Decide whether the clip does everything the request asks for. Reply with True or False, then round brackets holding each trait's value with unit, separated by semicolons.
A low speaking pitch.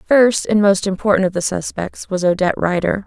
False (190 Hz)